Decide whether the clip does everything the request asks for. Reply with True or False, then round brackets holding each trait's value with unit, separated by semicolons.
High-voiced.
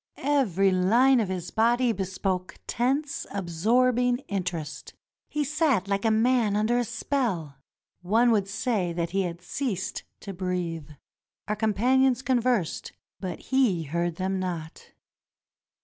True (205 Hz)